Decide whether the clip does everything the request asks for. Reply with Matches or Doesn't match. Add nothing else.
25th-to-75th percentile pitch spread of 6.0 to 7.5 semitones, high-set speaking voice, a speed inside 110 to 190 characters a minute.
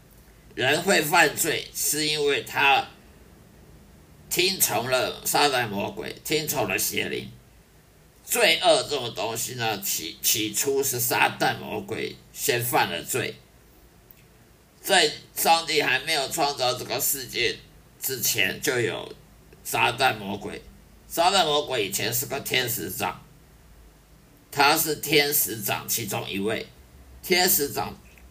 Doesn't match